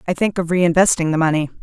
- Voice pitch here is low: No, medium, 170 Hz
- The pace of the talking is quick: Yes, fast, 220 wpm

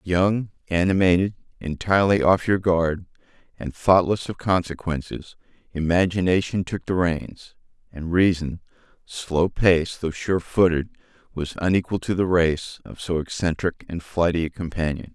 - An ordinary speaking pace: No, slow, 130 wpm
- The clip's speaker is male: Yes, male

